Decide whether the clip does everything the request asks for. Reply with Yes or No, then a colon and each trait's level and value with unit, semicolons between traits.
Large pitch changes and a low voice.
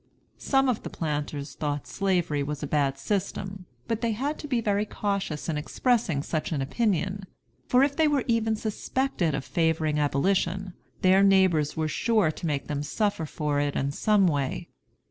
No: wide, 6.3 semitones; medium, 185 Hz